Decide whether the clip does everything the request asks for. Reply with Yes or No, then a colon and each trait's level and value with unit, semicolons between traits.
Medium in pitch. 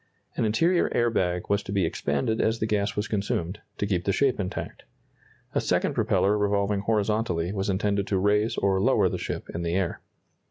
No: low, 100 Hz